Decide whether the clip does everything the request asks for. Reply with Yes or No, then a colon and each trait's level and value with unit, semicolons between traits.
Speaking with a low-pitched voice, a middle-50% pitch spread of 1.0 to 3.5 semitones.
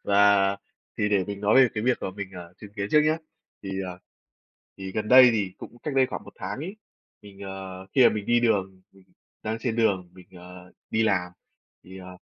Yes: low, 100 Hz; average, 3.2 semitones